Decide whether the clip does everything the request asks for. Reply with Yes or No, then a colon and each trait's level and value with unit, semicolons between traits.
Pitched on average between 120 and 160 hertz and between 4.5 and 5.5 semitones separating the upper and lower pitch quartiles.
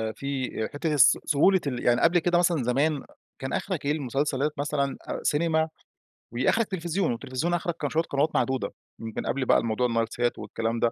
Yes: medium, 140 Hz; average, 4.8 semitones